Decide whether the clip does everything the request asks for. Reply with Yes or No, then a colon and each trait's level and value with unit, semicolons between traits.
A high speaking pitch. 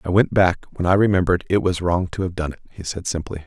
No: very low, 90 Hz